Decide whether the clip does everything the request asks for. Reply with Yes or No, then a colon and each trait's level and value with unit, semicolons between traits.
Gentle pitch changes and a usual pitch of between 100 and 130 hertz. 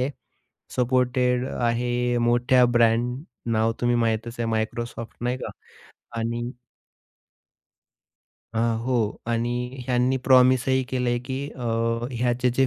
Yes: narrow, 1.2 semitones; low, 125 Hz